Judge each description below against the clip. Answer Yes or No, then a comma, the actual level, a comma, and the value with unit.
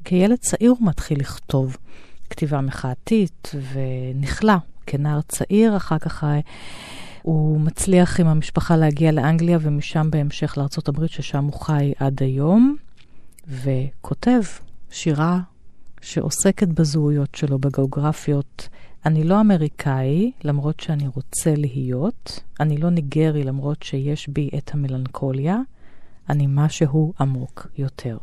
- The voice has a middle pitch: Yes, medium, 150 Hz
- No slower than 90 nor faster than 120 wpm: Yes, average, 105 wpm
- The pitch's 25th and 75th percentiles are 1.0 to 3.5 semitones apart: Yes, average, 3.1 semitones